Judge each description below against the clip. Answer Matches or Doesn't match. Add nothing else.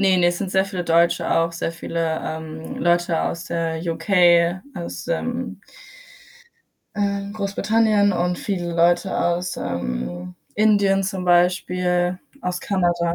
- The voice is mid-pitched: Matches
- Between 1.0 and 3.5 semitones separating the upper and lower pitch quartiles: Matches